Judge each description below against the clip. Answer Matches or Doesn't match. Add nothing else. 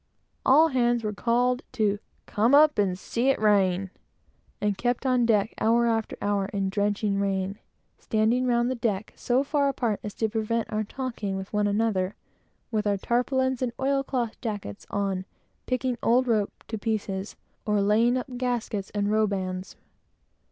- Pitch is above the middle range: Matches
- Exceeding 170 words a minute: Doesn't match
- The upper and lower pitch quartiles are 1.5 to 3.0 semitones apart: Doesn't match